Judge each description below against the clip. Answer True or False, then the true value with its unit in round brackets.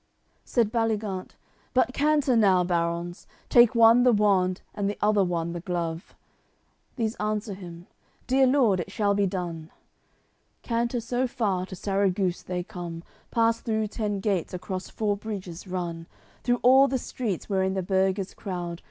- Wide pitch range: False (4.1 semitones)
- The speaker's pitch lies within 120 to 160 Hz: False (200 Hz)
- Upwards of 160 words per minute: False (155 wpm)